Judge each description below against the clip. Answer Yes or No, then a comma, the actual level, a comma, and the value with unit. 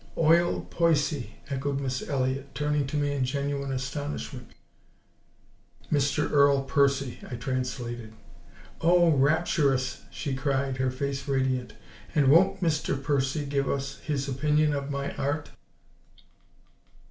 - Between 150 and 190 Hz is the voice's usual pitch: No, medium, 140 Hz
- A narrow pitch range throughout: Yes, narrow, 1.9 semitones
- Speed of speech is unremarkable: No, slow, 120 wpm